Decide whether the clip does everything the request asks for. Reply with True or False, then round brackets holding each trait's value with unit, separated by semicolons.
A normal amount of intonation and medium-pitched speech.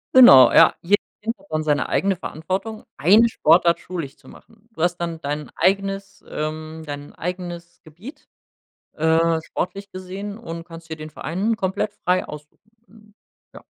True (3.9 semitones; 175 Hz)